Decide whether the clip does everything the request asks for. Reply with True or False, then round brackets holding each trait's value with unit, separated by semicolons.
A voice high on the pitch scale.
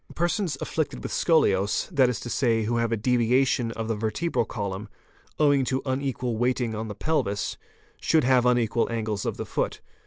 False (120 Hz)